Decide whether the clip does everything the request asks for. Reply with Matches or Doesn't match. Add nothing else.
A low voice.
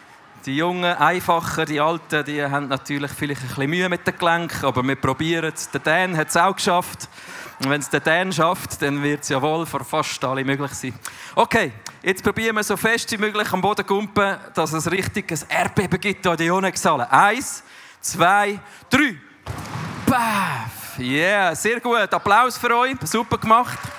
Doesn't match